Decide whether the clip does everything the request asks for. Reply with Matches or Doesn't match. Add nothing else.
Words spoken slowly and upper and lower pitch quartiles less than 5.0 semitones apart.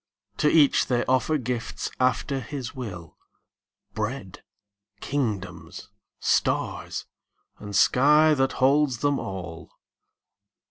Doesn't match